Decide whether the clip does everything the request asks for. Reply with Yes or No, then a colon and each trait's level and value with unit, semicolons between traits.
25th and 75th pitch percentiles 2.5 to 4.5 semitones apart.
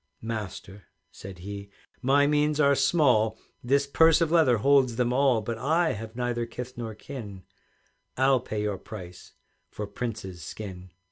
No: average, 5.1 semitones